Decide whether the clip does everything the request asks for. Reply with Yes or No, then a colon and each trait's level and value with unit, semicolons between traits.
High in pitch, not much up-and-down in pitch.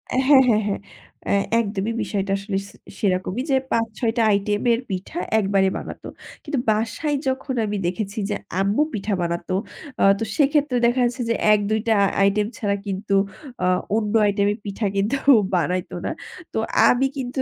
No: high, 210 Hz; average, 3.3 semitones